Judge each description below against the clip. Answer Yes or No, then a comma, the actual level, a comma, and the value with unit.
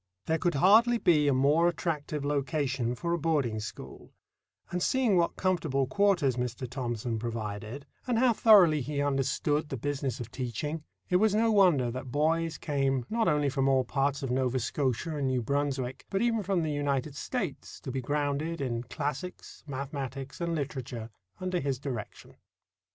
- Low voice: No, medium, 145 Hz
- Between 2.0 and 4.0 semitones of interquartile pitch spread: No, average, 4.4 semitones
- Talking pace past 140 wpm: Yes, average, 165 wpm